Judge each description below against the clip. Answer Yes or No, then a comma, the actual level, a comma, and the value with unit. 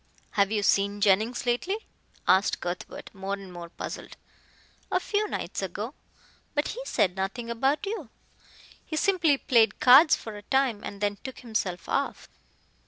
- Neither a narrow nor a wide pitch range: No, wide, 5.7 semitones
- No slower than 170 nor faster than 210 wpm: No, average, 155 wpm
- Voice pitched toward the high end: Yes, high, 225 Hz